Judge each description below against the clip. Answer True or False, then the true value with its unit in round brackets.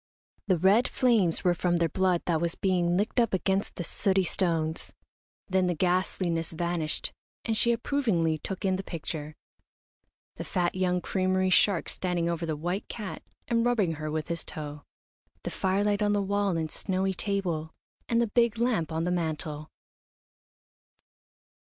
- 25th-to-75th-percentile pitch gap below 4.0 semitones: True (3.3 semitones)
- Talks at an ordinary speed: True (160 wpm)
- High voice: False (180 Hz)